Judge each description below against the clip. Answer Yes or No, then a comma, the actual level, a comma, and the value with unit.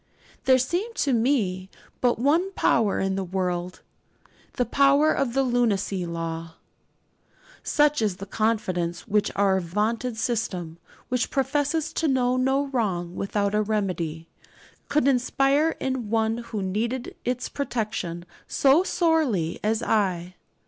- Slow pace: Yes, slow, 130 wpm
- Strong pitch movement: Yes, wide, 6.0 semitones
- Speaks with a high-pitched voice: Yes, high, 225 Hz